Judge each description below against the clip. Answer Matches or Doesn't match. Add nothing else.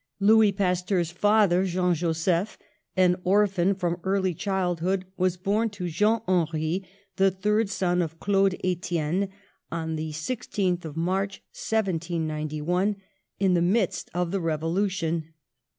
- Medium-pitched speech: Matches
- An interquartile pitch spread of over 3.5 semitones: Doesn't match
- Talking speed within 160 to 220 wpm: Doesn't match